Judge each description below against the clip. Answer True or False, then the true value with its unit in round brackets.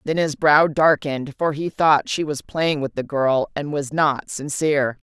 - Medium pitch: True (145 Hz)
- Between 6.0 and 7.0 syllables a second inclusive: False (4.3 syllables/s)